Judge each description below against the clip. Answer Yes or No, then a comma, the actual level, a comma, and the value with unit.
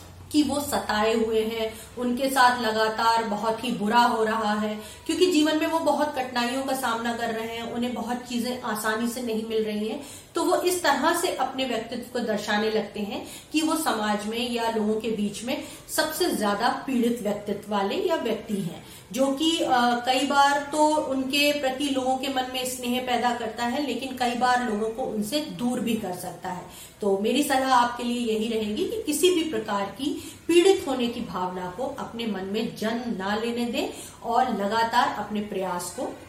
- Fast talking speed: Yes, fast, 195 wpm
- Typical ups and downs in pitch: Yes, average, 3.8 semitones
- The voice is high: Yes, high, 240 Hz